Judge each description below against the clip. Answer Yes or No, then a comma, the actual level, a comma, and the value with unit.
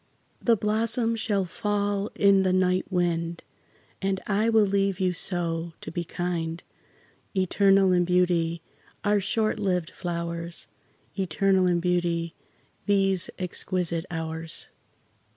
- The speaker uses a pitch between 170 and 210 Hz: Yes, medium, 185 Hz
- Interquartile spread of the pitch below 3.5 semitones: Yes, average, 2.7 semitones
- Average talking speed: No, slow, 115 wpm